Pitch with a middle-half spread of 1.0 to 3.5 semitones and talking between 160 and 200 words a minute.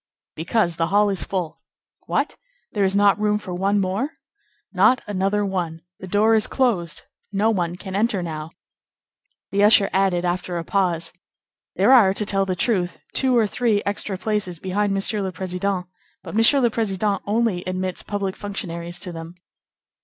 Yes: narrow, 2.6 semitones; average, 170 wpm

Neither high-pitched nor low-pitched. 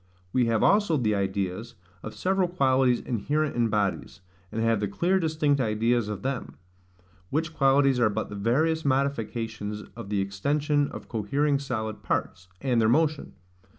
No: low, 120 Hz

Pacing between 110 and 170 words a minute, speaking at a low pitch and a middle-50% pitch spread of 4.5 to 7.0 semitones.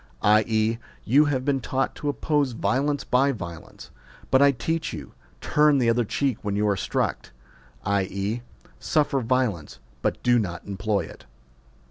Yes: average, 155 wpm; low, 120 Hz; average, 5.2 semitones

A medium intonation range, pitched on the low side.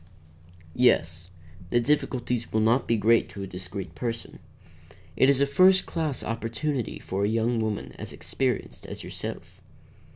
Yes: average, 3.6 semitones; low, 115 Hz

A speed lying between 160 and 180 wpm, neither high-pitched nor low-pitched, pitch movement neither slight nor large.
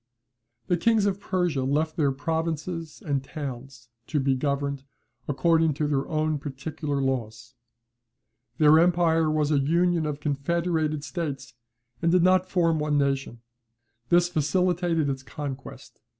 No: slow, 135 wpm; medium, 155 Hz; average, 3.3 semitones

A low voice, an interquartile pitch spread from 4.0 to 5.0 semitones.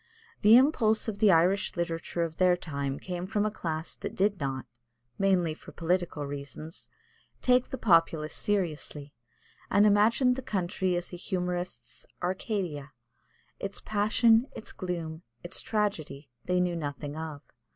No: medium, 180 Hz; average, 4.5 semitones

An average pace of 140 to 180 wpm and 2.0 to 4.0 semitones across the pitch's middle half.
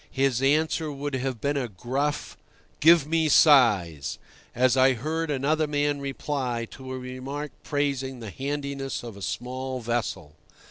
Yes: average, 145 wpm; average, 2.7 semitones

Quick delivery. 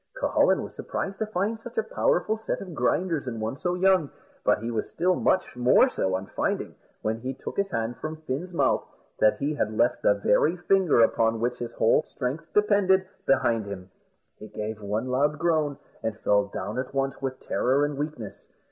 No: average, 195 wpm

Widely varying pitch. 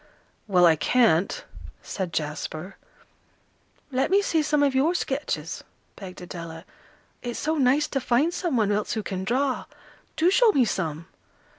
Yes: wide, 8.4 semitones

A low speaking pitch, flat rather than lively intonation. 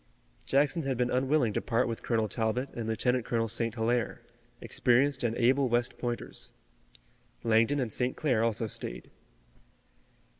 Yes: low, 120 Hz; narrow, 2.2 semitones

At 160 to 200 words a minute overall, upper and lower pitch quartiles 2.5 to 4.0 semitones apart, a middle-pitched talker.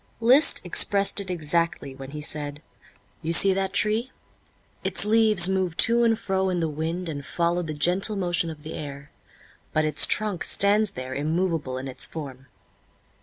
No: average, 170 wpm; average, 4.7 semitones; medium, 170 Hz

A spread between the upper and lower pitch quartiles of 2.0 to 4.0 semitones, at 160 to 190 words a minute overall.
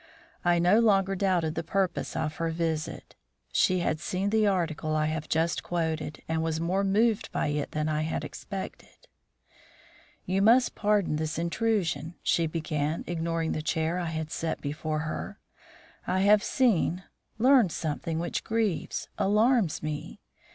No: average, 3.7 semitones; average, 150 wpm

